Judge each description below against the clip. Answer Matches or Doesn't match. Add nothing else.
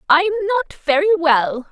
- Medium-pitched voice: Doesn't match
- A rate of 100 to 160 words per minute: Matches